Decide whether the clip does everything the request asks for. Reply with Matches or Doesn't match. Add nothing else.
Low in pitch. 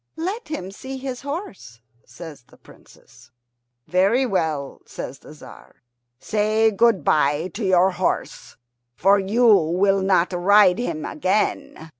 Doesn't match